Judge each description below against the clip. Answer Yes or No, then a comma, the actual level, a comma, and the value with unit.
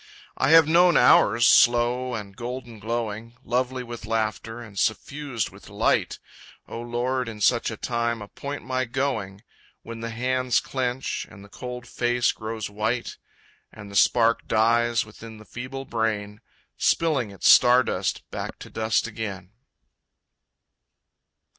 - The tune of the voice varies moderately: No, narrow, 2.3 semitones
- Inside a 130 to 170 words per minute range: Yes, average, 140 wpm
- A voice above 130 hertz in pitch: No, low, 120 Hz